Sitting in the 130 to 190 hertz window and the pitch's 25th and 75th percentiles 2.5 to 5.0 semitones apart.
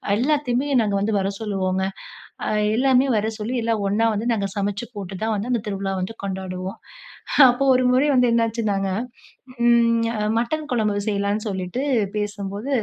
No: high, 215 Hz; average, 3.2 semitones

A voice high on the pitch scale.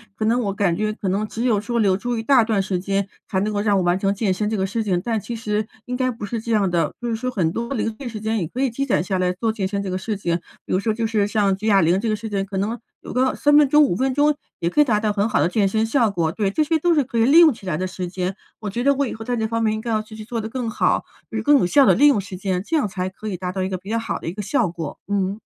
Yes: high, 215 Hz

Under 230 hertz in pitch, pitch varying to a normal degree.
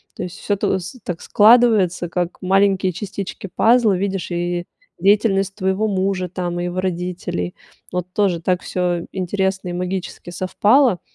No: medium, 185 Hz; narrow, 2.0 semitones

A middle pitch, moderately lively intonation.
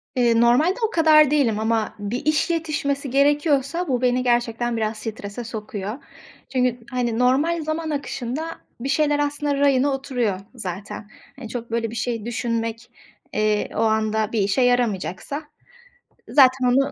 No: high, 245 Hz; average, 4.0 semitones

